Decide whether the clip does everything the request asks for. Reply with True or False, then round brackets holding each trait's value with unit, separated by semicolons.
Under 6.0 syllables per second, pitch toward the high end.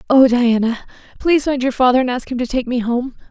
False (6.2 syllables/s; 250 Hz)